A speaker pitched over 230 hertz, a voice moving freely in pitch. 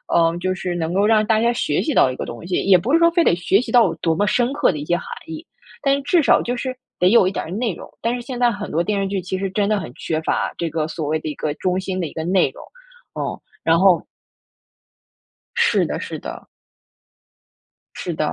No: high, 190 Hz; wide, 5.8 semitones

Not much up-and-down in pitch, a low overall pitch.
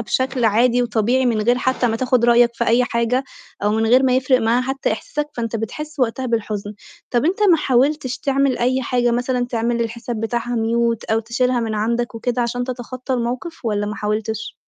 No: narrow, 2.1 semitones; high, 240 Hz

